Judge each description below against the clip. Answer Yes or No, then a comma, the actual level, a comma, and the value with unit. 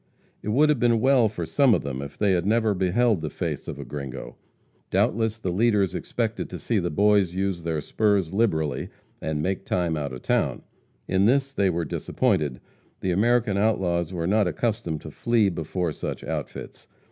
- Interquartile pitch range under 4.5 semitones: No, average, 5.1 semitones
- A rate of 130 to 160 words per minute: No, average, 185 wpm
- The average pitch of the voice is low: Yes, very low, 95 Hz